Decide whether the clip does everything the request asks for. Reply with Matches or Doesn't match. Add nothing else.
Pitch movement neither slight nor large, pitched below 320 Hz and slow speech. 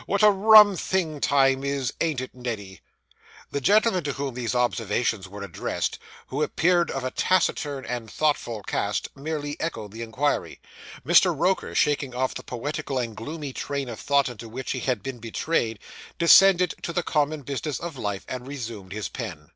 Doesn't match